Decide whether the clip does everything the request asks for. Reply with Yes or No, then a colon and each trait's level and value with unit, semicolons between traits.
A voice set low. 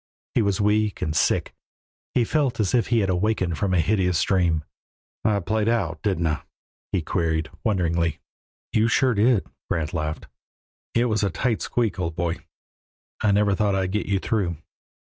Yes: low, 100 Hz